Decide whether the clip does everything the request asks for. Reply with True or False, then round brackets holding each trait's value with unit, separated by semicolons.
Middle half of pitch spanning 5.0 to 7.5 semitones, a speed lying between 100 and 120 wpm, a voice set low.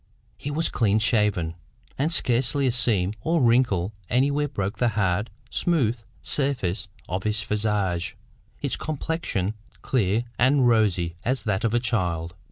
False (5.3 semitones; 140 wpm; 110 Hz)